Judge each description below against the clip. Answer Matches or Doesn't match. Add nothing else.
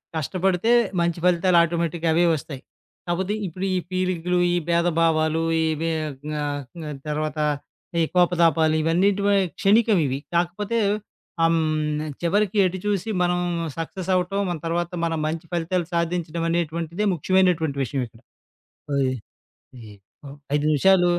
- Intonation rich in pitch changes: Doesn't match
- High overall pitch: Doesn't match